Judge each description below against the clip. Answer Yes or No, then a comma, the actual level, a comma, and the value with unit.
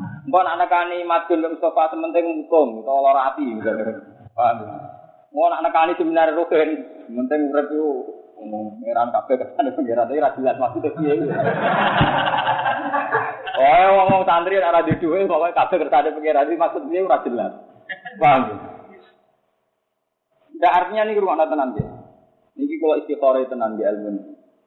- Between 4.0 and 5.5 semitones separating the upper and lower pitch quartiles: Yes, average, 4.5 semitones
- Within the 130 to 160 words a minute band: Yes, average, 135 wpm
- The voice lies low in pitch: No, medium, 165 Hz